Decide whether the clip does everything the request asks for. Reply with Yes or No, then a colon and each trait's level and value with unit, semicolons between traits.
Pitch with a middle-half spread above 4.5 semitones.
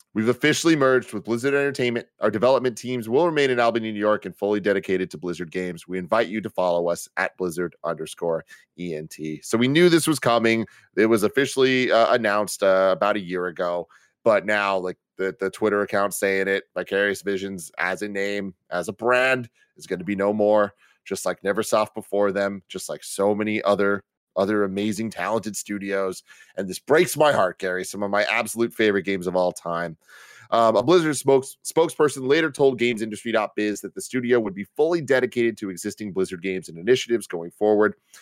No: average, 3.7 semitones